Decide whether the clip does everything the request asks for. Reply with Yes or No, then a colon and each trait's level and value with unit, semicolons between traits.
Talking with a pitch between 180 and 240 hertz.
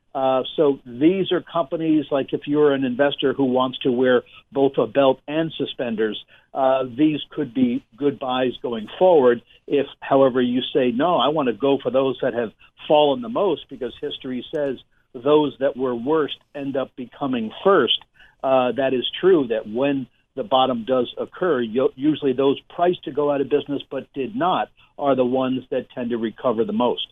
No: low, 135 Hz